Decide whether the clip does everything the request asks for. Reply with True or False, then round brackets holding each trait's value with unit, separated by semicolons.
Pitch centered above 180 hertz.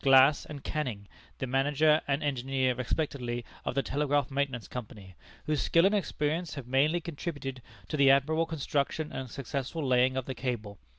False (135 Hz)